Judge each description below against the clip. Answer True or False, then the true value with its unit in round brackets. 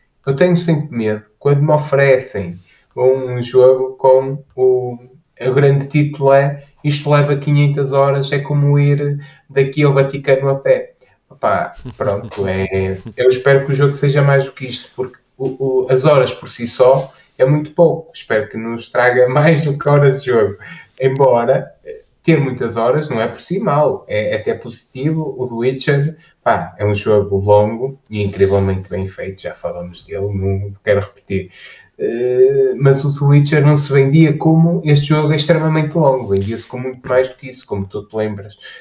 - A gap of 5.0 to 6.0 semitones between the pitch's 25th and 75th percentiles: False (3.8 semitones)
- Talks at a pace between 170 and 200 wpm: True (180 wpm)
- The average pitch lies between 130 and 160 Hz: True (135 Hz)